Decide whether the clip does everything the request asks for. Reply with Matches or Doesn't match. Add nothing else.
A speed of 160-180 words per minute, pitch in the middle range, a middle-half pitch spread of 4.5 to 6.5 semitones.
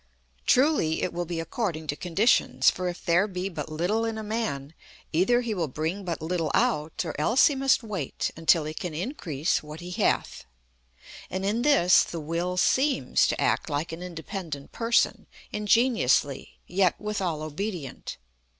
Matches